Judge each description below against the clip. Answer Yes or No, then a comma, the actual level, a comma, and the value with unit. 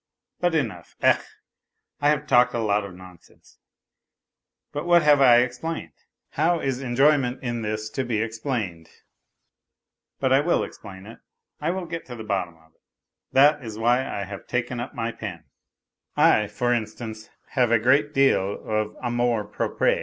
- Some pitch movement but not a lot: Yes, average, 4.4 semitones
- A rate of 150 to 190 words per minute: Yes, average, 165 wpm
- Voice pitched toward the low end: Yes, low, 120 Hz